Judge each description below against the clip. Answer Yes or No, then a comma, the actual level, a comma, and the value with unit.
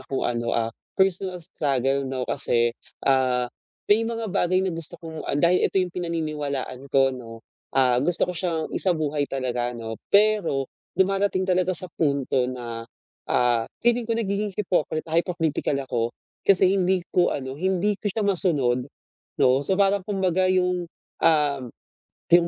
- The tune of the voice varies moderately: No, wide, 6.0 semitones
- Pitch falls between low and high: Yes, medium, 165 Hz